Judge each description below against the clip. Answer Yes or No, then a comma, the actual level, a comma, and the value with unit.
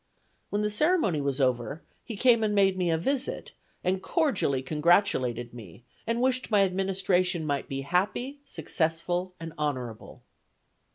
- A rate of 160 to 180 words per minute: No, average, 145 wpm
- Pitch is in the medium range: Yes, medium, 180 Hz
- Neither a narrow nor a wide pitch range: No, wide, 6.8 semitones